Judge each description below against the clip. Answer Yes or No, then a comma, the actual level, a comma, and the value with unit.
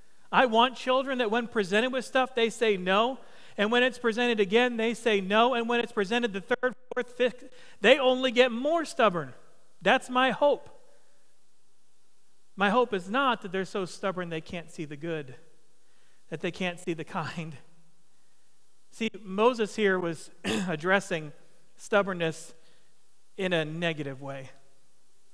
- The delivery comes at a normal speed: Yes, average, 150 wpm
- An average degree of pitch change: No, wide, 6.4 semitones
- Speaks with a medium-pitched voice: No, high, 205 Hz